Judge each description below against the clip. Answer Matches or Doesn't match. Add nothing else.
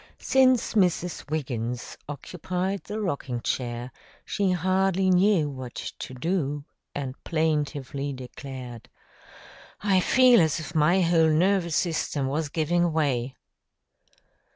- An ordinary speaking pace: Doesn't match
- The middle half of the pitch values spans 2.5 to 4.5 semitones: Doesn't match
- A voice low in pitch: Doesn't match